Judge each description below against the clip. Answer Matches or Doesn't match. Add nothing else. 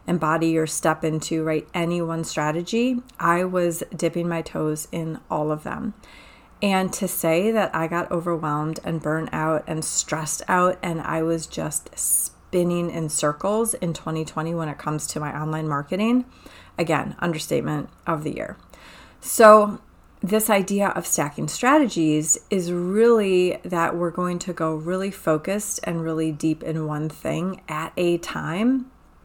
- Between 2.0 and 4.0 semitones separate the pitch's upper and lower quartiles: Matches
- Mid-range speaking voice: Matches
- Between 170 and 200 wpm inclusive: Doesn't match